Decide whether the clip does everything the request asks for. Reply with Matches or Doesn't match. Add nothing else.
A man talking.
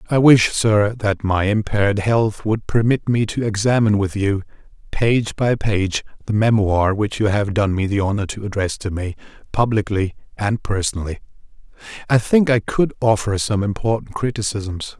Matches